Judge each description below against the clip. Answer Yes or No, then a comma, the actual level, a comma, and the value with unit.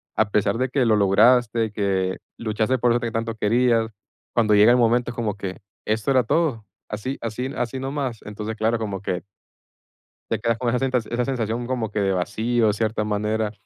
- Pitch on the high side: No, low, 115 Hz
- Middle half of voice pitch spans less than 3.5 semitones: Yes, narrow, 2.5 semitones